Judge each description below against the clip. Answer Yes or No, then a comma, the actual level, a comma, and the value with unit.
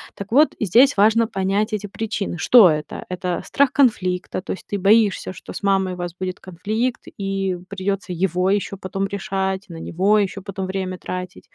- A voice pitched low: No, high, 195 Hz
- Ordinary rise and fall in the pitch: No, narrow, 2.2 semitones